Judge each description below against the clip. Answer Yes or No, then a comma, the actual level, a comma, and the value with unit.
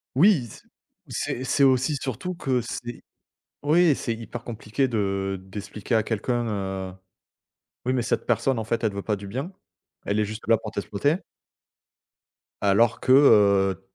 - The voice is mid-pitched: No, low, 115 Hz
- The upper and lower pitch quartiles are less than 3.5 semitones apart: No, average, 4.1 semitones